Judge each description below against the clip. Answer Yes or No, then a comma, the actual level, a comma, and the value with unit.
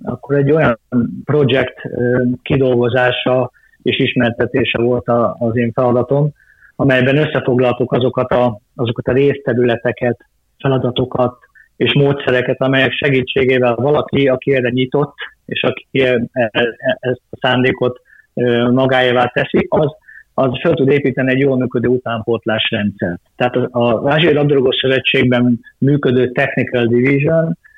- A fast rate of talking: No, average, 110 wpm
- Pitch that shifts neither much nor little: No, narrow, 1.8 semitones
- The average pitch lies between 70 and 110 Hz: No, low, 125 Hz